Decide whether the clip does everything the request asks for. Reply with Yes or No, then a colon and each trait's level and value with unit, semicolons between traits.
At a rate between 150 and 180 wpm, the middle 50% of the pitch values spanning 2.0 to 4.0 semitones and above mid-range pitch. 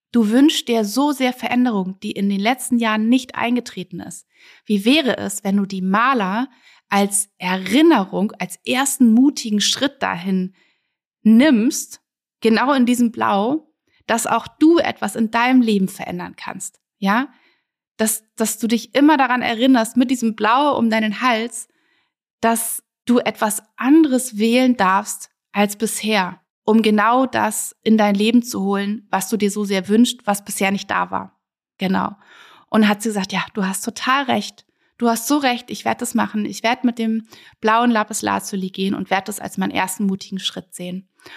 Yes: average, 170 wpm; average, 3.7 semitones; high, 225 Hz